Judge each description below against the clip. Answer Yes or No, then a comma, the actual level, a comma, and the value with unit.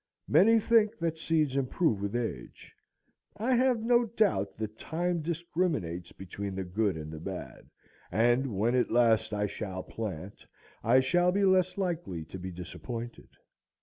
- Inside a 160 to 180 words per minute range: No, average, 150 wpm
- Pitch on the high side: No, low, 120 Hz